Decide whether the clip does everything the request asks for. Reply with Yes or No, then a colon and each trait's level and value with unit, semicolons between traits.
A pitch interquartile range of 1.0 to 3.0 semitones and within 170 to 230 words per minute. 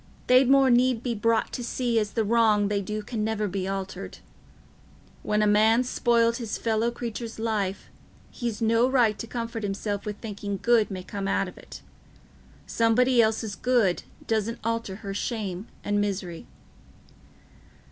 No: narrow, 2.4 semitones; average, 155 wpm